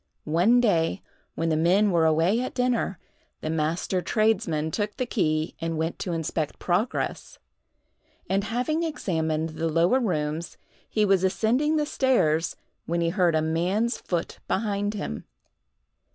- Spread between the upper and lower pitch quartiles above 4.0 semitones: Yes, average, 5.2 semitones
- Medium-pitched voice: Yes, medium, 180 Hz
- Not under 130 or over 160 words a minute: Yes, average, 145 wpm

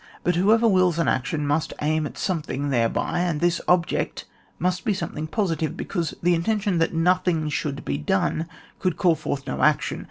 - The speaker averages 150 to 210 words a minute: Yes, average, 185 wpm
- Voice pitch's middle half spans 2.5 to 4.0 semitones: Yes, average, 3.2 semitones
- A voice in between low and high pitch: Yes, medium, 165 Hz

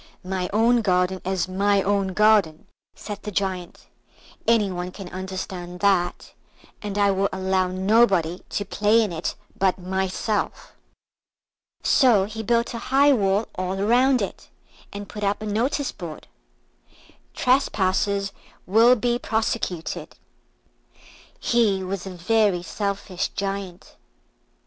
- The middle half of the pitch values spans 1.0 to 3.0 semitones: Yes, average, 2.7 semitones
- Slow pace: Yes, slow, 125 wpm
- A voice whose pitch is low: No, high, 200 Hz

